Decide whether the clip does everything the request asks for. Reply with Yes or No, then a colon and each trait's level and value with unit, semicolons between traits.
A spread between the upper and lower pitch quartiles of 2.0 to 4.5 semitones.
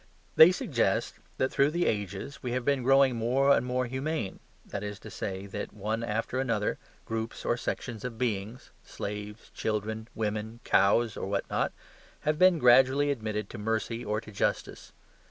Yes: average, 3.7 semitones